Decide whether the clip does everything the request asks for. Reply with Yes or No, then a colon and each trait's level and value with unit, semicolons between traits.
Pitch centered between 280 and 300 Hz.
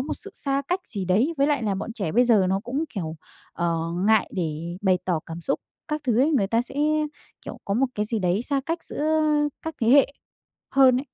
No: high, 230 Hz